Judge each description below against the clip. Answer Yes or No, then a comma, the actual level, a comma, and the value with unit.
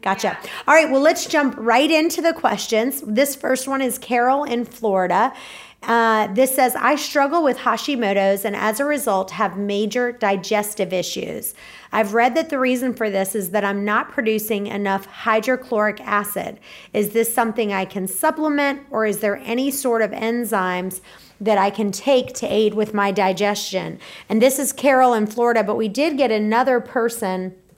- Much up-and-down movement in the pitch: No, average, 4.1 semitones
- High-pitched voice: Yes, high, 225 Hz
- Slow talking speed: No, average, 175 wpm